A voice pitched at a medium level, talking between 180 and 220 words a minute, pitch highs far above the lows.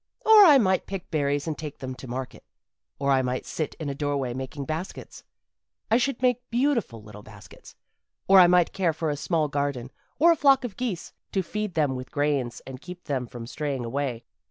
Yes: medium, 150 Hz; fast, 205 wpm; wide, 6.6 semitones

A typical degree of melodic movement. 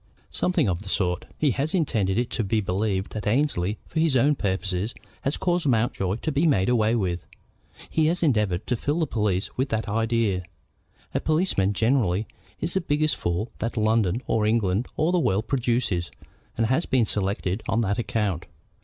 No: wide, 6.0 semitones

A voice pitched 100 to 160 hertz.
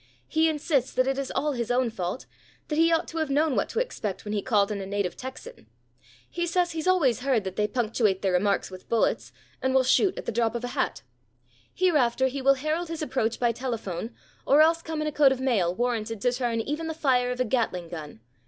No: very high, 255 Hz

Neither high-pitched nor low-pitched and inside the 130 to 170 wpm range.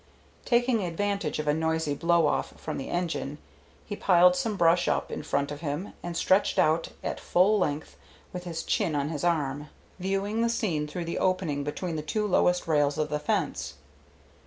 No: medium, 170 Hz; average, 185 wpm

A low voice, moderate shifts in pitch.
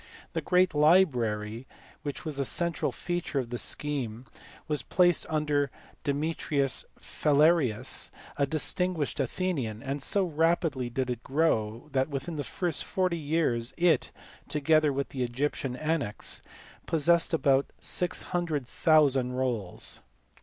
No: medium, 145 Hz; average, 4.1 semitones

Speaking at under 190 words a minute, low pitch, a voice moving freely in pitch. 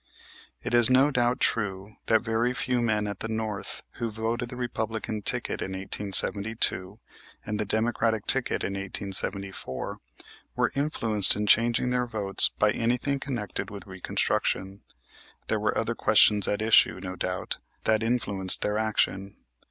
No: average, 145 wpm; low, 110 Hz; average, 3.1 semitones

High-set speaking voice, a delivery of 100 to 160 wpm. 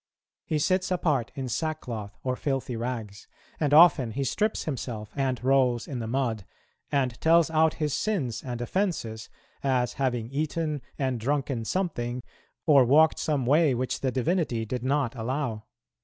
No: low, 135 Hz; average, 155 wpm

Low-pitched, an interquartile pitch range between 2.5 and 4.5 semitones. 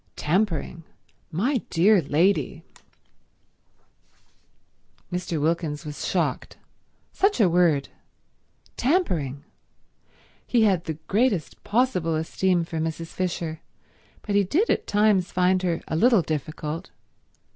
No: medium, 180 Hz; average, 4.2 semitones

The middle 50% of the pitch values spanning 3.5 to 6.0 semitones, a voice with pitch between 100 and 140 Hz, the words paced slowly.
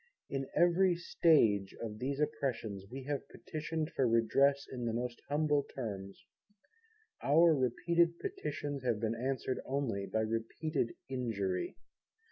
Yes: average, 4.9 semitones; low, 135 Hz; slow, 125 wpm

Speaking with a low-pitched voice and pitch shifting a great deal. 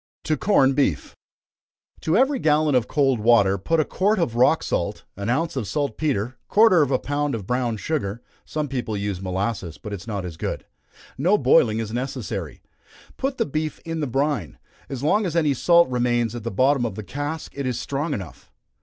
Yes: low, 130 Hz; wide, 5.7 semitones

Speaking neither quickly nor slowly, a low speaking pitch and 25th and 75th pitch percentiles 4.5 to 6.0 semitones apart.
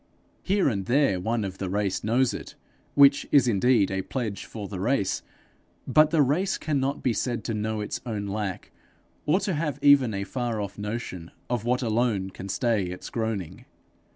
Yes: average, 180 wpm; low, 115 Hz; average, 5.1 semitones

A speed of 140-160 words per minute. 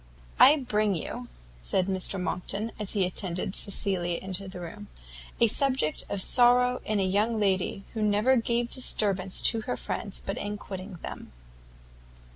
Yes: average, 155 wpm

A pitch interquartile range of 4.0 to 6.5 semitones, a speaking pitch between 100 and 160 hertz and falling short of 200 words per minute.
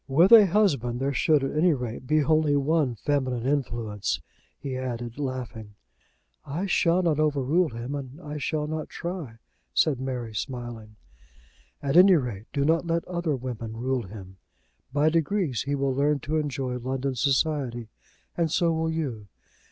Yes: average, 4.3 semitones; medium, 140 Hz; average, 160 wpm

